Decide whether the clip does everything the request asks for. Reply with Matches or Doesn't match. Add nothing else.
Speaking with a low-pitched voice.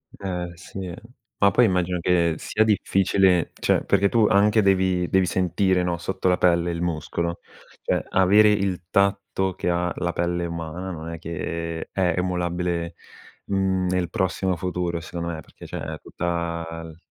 Matches